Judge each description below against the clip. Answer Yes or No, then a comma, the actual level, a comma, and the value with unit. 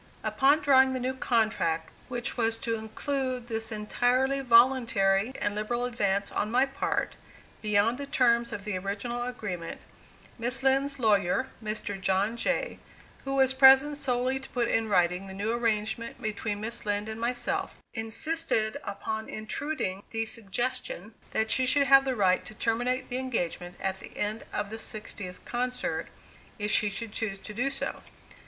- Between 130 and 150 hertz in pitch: No, high, 230 Hz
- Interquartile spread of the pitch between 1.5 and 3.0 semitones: No, average, 3.7 semitones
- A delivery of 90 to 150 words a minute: No, average, 160 wpm